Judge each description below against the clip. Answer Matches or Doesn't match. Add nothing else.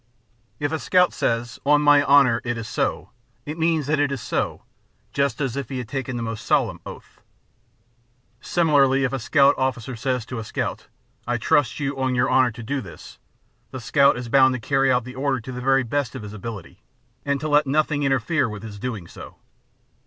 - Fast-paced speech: Matches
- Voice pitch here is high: Doesn't match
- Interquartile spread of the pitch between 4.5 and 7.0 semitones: Doesn't match